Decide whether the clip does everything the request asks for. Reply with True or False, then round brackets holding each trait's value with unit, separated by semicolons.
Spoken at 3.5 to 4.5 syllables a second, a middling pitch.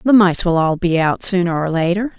False (5.4 syllables/s; 180 Hz)